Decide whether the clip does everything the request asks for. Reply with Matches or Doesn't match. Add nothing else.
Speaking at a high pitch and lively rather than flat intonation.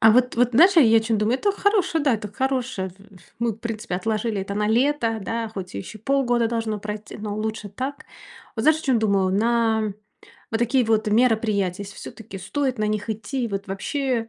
Doesn't match